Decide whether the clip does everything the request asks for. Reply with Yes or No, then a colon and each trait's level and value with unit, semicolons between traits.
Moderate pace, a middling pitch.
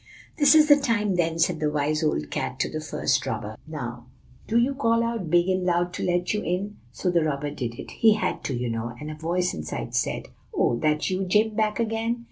No: fast, 230 wpm; medium, 175 Hz